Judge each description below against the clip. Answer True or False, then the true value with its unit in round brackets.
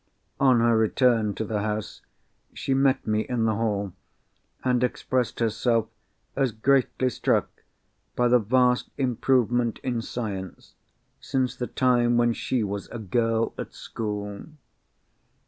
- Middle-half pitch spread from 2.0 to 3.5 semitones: True (2.6 semitones)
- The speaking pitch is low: True (120 Hz)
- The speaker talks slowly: True (130 wpm)